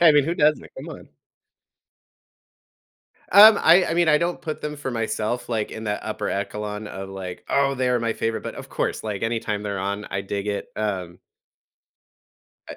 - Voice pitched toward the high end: No, low, 110 Hz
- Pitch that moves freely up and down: Yes, wide, 6.2 semitones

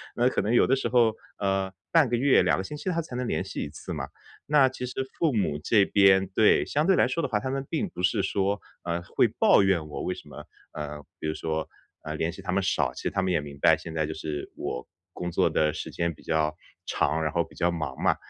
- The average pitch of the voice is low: Yes, very low, 95 Hz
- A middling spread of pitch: No, wide, 7.7 semitones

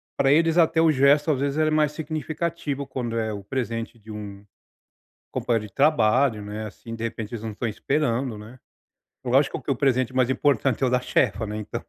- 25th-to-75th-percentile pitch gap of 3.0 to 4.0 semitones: No, average, 4.6 semitones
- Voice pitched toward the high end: No, low, 130 Hz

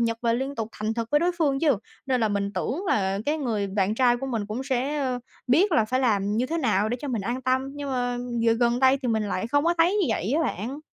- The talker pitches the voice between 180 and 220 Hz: No, high, 245 Hz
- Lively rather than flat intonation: No, average, 4.1 semitones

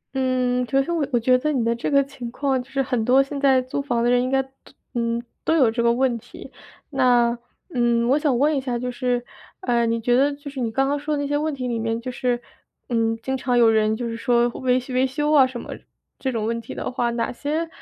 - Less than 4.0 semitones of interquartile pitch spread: Yes, narrow, 2.5 semitones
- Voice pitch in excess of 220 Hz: Yes, very high, 250 Hz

